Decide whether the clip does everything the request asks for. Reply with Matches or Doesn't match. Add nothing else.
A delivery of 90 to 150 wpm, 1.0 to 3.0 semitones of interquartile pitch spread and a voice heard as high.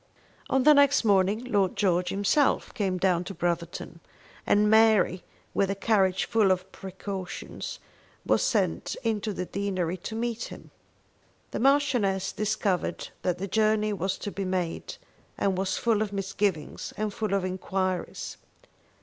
Matches